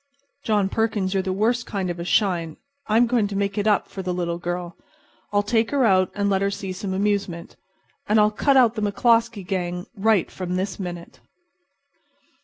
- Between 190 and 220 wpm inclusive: Yes, average, 195 wpm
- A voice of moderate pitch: No, high, 200 Hz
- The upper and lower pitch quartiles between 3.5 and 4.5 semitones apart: No, average, 2.8 semitones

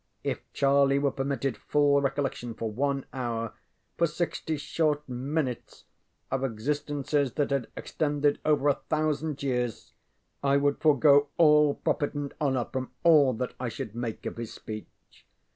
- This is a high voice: No, medium, 140 Hz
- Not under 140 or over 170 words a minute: Yes, average, 145 wpm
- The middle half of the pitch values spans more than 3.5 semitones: No, narrow, 2.4 semitones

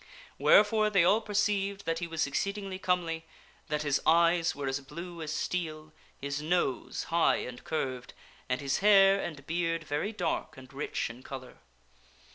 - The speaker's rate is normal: Yes, average, 160 wpm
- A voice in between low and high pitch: Yes, medium, 165 Hz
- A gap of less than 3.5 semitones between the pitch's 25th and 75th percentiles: No, average, 4.6 semitones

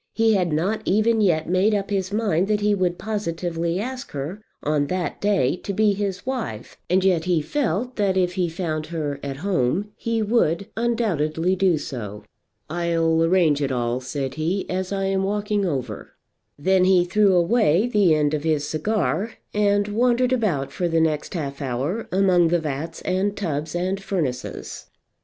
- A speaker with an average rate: Yes, average, 170 wpm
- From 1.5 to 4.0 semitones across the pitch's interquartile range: No, average, 4.7 semitones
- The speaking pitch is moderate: Yes, medium, 180 Hz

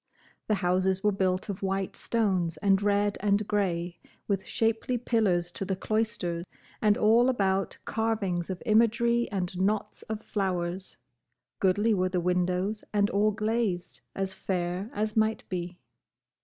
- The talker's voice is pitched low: No, high, 195 Hz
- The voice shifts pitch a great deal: No, average, 2.9 semitones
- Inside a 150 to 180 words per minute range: No, average, 140 wpm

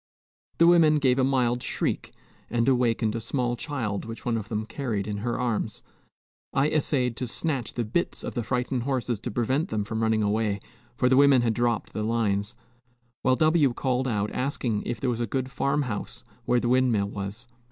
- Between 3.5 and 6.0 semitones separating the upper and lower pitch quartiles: No, average, 3.0 semitones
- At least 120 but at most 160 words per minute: No, average, 195 wpm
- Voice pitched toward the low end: Yes, low, 120 Hz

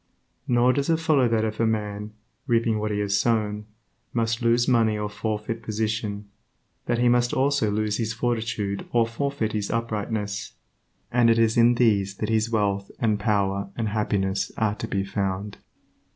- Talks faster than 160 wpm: Yes, average, 170 wpm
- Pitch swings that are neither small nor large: No, narrow, 2.1 semitones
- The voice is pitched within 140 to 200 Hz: No, low, 110 Hz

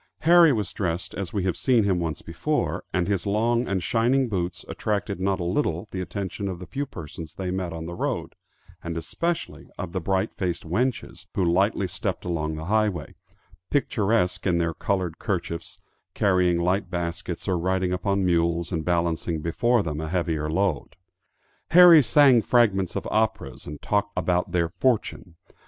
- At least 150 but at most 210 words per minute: Yes, average, 170 wpm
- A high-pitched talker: No, very low, 90 Hz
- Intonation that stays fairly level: No, average, 3.4 semitones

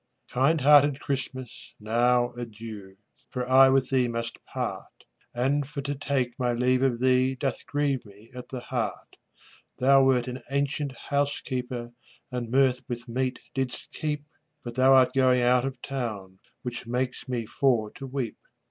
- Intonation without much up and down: Yes, narrow, 1.9 semitones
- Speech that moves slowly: No, average, 155 wpm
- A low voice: Yes, low, 130 Hz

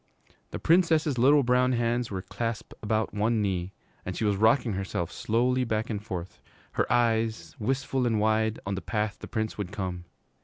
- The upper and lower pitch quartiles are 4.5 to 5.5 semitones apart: No, average, 3.2 semitones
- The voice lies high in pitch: No, low, 110 Hz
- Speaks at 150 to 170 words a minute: No, average, 180 wpm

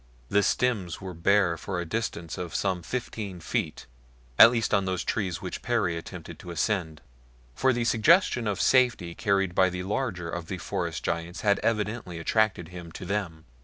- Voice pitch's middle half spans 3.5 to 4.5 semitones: Yes, average, 4.0 semitones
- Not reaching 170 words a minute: No, average, 175 wpm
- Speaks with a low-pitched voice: Yes, very low, 95 Hz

